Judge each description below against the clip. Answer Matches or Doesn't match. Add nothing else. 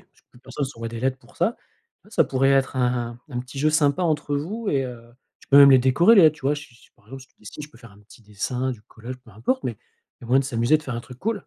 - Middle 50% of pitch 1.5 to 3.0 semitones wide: Doesn't match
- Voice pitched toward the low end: Matches